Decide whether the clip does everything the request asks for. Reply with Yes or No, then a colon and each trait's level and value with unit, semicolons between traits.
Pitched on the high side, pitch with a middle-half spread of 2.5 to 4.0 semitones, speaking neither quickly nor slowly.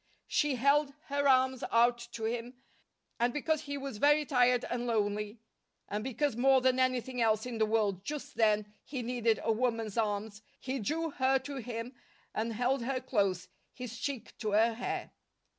Yes: high, 245 Hz; average, 3.1 semitones; average, 175 wpm